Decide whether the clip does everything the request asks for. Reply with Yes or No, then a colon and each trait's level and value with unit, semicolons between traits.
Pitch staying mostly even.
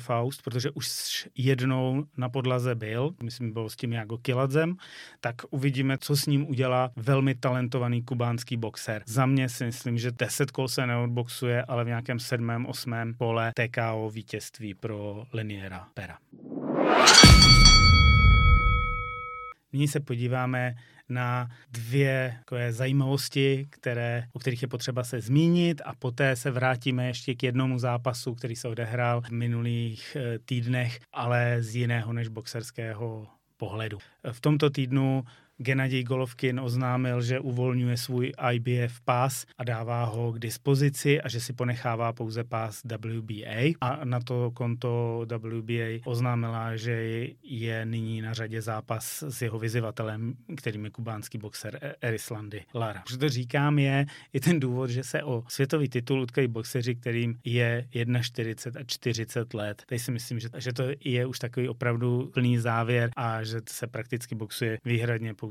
Yes: narrow, 2.1 semitones